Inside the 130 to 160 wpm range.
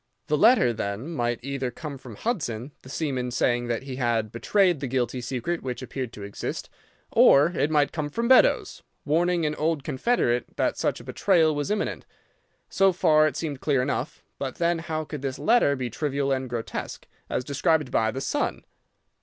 No: average, 185 wpm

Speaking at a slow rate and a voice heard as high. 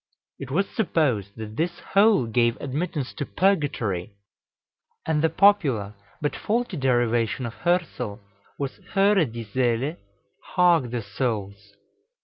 No: slow, 125 wpm; low, 130 Hz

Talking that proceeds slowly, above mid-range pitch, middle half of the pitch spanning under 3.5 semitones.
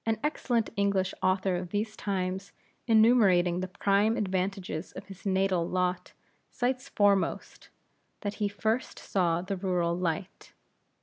Yes: slow, 130 wpm; high, 195 Hz; narrow, 2.5 semitones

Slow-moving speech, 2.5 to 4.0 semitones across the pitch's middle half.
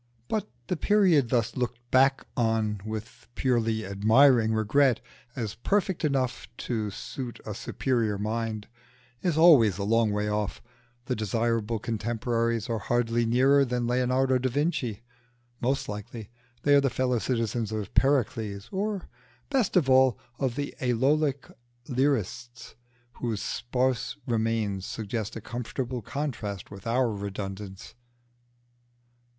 Yes: slow, 130 wpm; average, 3.2 semitones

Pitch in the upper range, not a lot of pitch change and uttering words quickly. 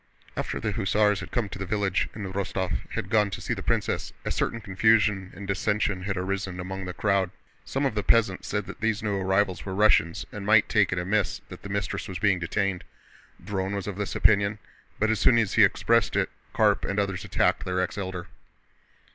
No: low, 100 Hz; narrow, 1.9 semitones; fast, 210 wpm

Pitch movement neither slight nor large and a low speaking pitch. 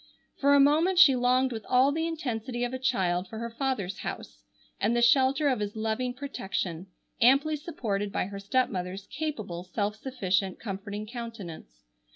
No: average, 5.0 semitones; high, 235 Hz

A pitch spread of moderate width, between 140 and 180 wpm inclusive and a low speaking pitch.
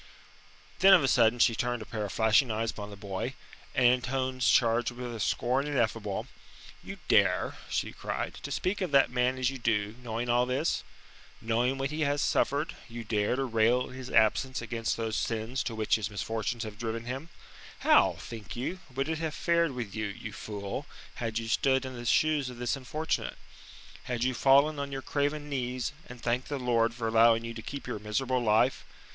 No: average, 3.0 semitones; average, 200 wpm; low, 120 Hz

